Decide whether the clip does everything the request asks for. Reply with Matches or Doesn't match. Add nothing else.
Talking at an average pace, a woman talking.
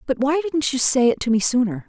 Doesn't match